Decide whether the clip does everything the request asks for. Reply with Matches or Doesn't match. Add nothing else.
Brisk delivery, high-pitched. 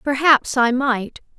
Doesn't match